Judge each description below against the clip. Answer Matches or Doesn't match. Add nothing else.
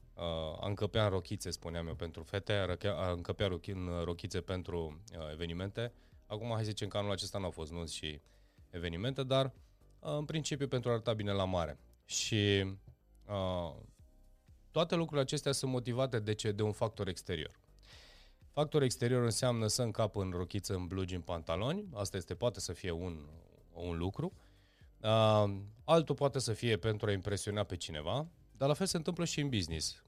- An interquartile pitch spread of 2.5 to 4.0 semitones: Doesn't match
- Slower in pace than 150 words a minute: Doesn't match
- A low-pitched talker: Matches